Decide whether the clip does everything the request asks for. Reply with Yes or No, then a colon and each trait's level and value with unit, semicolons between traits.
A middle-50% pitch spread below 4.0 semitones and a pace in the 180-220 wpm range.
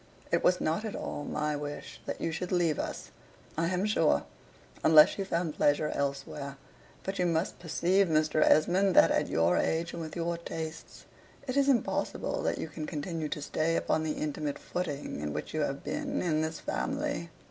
Yes: average, 3.0 semitones; average, 190 wpm